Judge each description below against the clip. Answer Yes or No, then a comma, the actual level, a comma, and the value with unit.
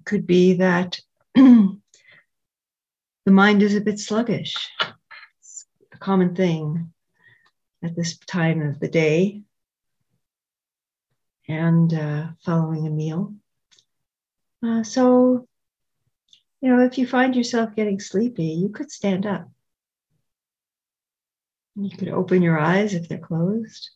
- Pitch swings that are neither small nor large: Yes, average, 4.5 semitones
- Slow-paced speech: Yes, slow, 115 wpm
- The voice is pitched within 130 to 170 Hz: No, high, 190 Hz